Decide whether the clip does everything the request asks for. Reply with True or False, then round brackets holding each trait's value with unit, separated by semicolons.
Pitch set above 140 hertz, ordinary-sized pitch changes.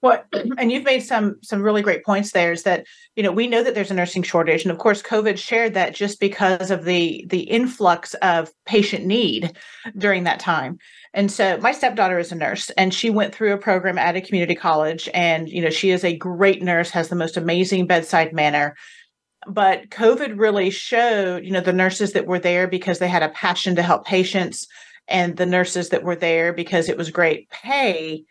True (185 Hz; 3.2 semitones)